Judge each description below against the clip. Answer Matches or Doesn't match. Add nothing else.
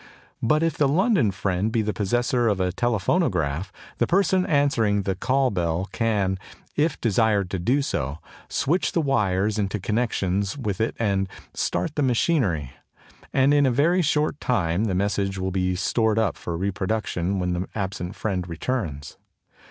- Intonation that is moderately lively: Doesn't match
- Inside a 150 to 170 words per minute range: Matches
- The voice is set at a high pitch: Doesn't match